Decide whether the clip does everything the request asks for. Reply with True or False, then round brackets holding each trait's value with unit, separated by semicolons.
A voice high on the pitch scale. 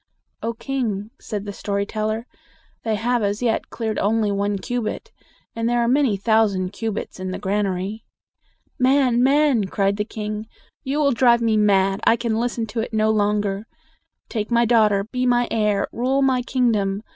True (220 Hz)